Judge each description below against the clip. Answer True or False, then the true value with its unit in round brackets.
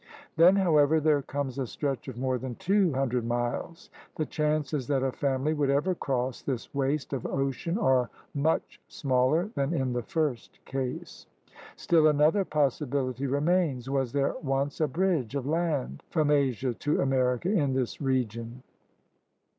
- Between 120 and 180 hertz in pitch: True (140 Hz)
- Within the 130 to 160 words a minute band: True (155 wpm)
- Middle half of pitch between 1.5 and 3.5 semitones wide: True (3.0 semitones)